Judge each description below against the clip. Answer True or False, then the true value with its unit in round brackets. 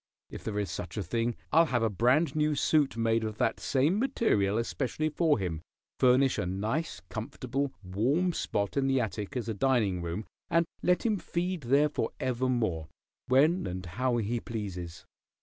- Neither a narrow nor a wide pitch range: False (6.1 semitones)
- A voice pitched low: True (120 Hz)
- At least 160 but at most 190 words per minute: True (170 wpm)